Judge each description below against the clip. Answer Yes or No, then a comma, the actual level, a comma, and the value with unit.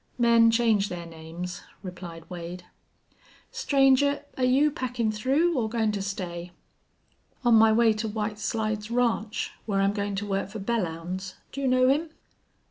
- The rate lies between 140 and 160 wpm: Yes, average, 155 wpm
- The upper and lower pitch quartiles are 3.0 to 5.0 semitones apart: Yes, average, 4.3 semitones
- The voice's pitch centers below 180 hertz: No, high, 215 Hz